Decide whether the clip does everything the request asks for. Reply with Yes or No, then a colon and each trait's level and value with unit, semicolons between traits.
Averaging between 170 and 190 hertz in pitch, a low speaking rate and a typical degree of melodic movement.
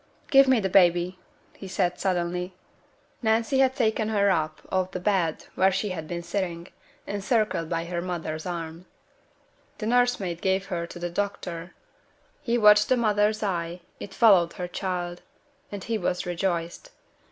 No: medium, 185 Hz; average, 150 wpm; average, 3.3 semitones